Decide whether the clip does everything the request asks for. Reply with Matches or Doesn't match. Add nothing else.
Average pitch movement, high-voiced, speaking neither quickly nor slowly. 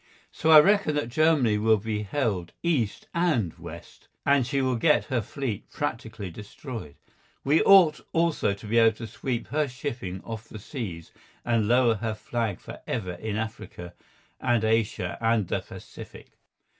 Doesn't match